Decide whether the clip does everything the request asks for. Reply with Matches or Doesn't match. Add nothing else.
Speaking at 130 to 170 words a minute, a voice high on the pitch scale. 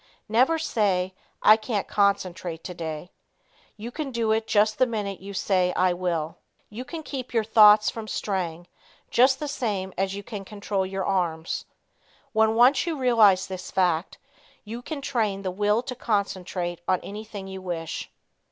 Matches